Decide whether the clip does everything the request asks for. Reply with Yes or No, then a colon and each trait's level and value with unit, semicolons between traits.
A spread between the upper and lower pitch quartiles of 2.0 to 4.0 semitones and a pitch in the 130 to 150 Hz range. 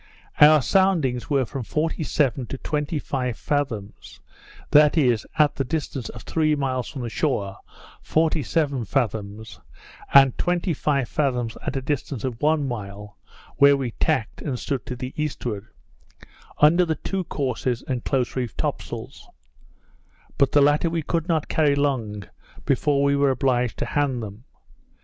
Yes: average, 3.6 semitones; low, 135 Hz